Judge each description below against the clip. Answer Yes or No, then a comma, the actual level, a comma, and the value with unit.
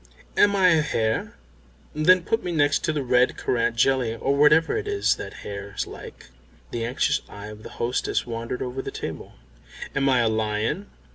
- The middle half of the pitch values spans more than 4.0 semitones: Yes, average, 5.1 semitones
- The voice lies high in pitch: No, low, 130 Hz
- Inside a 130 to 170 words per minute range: No, average, 185 wpm